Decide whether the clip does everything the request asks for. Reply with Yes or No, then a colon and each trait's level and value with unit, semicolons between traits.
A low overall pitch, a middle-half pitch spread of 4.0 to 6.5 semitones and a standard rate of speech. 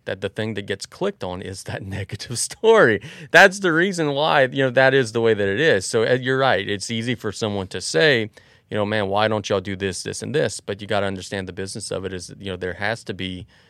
No: low, 105 Hz; average, 4.3 semitones; fast, 265 wpm